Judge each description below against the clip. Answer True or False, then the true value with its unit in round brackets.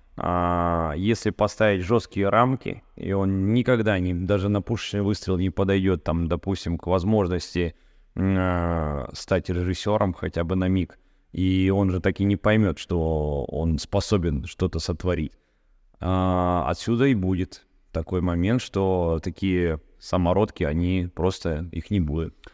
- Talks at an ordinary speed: True (140 wpm)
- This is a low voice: True (90 Hz)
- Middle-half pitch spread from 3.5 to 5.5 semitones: False (2.6 semitones)